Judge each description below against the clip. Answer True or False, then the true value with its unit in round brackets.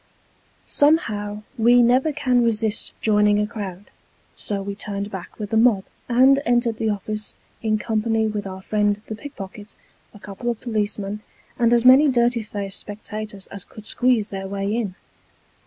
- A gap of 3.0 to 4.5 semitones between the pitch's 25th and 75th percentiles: False (2.6 semitones)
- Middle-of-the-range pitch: False (215 Hz)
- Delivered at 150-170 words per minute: True (160 wpm)